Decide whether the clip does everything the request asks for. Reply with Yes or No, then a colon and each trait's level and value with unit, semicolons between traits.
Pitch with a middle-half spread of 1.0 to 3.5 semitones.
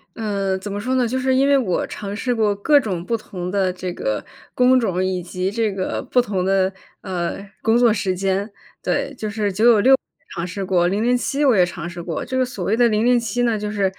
No: average, 4.3 semitones